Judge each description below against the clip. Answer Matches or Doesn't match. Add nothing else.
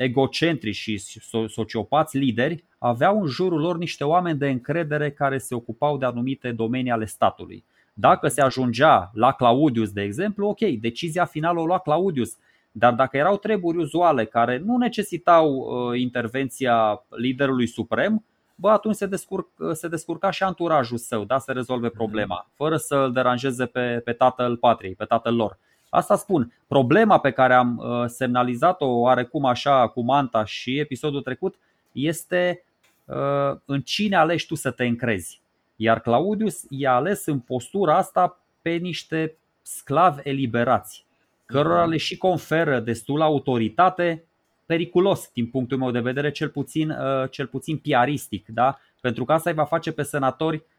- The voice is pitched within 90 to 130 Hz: Doesn't match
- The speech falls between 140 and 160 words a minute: Matches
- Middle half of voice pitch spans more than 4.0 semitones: Matches